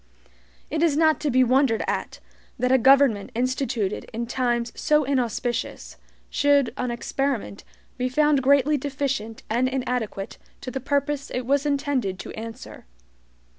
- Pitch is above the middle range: Yes, very high, 260 Hz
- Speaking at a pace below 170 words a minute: Yes, average, 140 wpm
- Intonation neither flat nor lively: Yes, average, 3.0 semitones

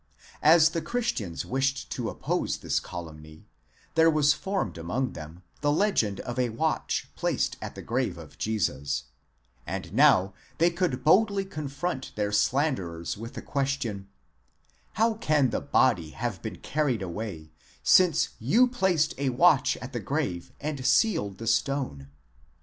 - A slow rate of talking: No, average, 145 wpm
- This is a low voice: Yes, low, 130 Hz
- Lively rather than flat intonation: Yes, wide, 7.6 semitones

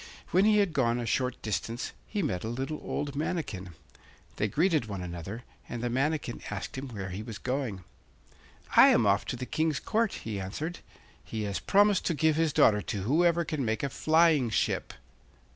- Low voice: Yes, low, 130 Hz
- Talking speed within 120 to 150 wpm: No, average, 190 wpm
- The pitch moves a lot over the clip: Yes, wide, 6.9 semitones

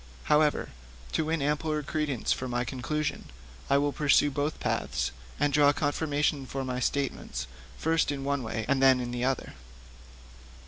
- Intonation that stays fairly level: Yes, narrow, 2.3 semitones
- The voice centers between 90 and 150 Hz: Yes, medium, 140 Hz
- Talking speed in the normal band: Yes, average, 155 wpm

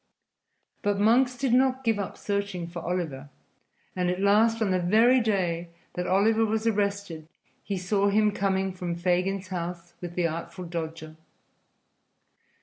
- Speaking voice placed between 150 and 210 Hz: Yes, high, 190 Hz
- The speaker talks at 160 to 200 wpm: No, average, 145 wpm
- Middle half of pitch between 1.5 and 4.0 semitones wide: Yes, average, 3.4 semitones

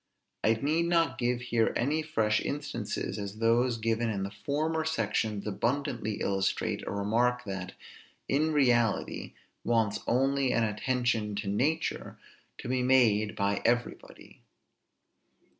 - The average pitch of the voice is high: No, low, 120 Hz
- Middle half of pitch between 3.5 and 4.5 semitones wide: Yes, average, 3.9 semitones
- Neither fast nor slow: No, slow, 125 wpm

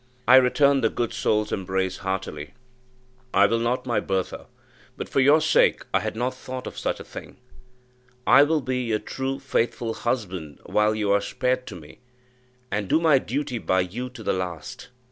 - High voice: No, low, 115 Hz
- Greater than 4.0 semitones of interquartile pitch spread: Yes, average, 5.0 semitones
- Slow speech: No, average, 185 wpm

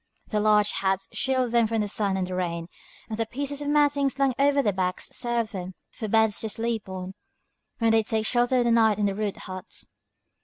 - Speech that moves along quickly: Yes, fast, 215 wpm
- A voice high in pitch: Yes, high, 220 Hz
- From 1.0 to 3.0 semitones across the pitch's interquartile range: No, average, 3.8 semitones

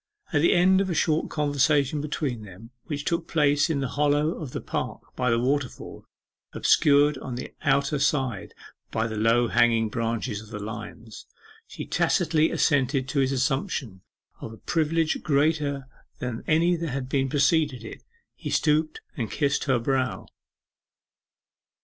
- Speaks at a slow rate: No, average, 155 wpm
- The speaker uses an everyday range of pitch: Yes, average, 4.0 semitones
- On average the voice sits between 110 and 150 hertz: Yes, medium, 140 Hz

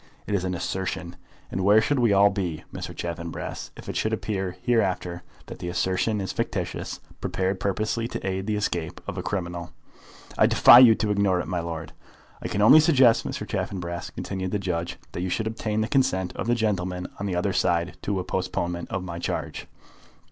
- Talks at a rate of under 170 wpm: No, average, 200 wpm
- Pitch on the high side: No, very low, 95 Hz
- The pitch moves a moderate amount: Yes, average, 3.2 semitones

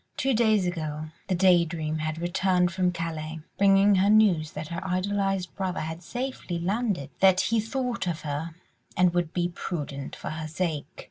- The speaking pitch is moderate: Yes, medium, 175 Hz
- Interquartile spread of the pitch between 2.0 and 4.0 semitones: Yes, average, 3.5 semitones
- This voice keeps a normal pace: Yes, average, 175 wpm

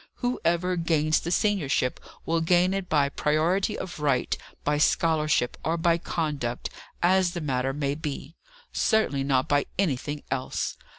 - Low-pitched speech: No, medium, 155 Hz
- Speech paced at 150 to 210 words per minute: No, average, 140 wpm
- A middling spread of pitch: Yes, average, 3.6 semitones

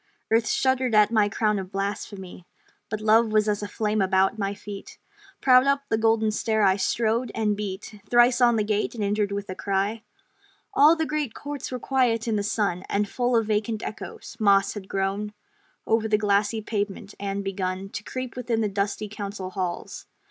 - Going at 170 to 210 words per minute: Yes, average, 190 wpm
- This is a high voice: Yes, high, 210 Hz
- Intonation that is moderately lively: No, narrow, 2.2 semitones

